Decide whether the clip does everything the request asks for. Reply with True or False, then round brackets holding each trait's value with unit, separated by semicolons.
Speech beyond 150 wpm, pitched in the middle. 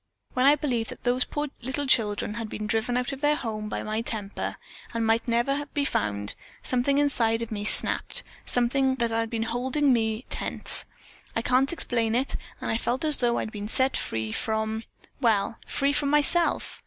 False (190 wpm; 235 Hz)